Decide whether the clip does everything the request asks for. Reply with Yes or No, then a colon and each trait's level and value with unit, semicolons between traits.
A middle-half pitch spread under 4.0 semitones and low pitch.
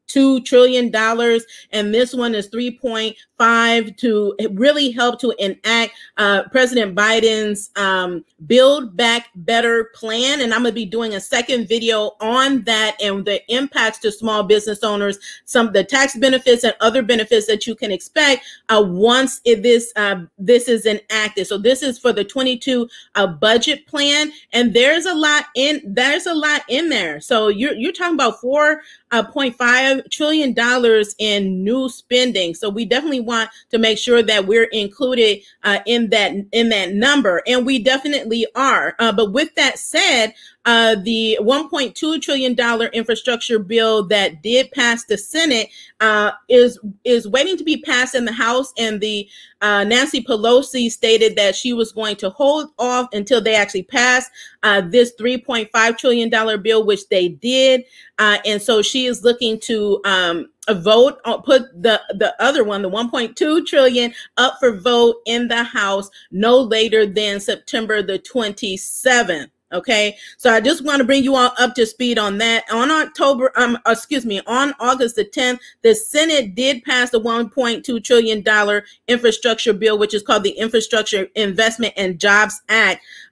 No: average, 3.1 semitones; high, 230 Hz